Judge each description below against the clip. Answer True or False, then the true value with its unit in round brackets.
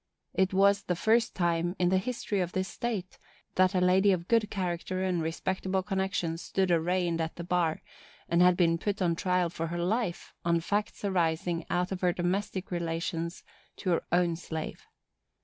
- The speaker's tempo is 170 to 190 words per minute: True (180 wpm)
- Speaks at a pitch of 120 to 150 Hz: False (180 Hz)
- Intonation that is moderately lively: False (2.0 semitones)